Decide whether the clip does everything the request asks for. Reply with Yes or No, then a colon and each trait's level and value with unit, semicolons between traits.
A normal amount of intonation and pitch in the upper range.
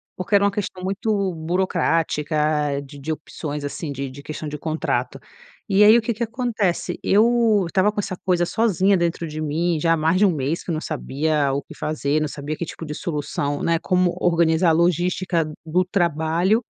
No: average, 3.8 semitones; medium, 170 Hz